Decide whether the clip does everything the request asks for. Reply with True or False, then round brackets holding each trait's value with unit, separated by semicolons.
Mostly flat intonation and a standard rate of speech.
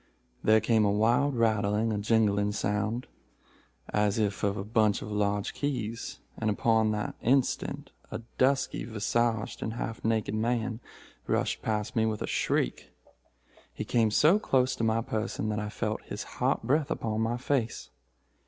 True (1.9 semitones; 160 wpm)